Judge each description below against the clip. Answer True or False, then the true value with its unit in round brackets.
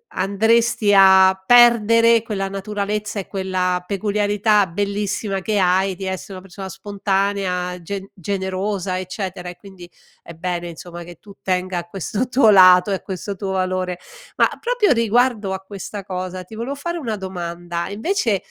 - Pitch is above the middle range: True (195 Hz)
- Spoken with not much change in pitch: True (2.3 semitones)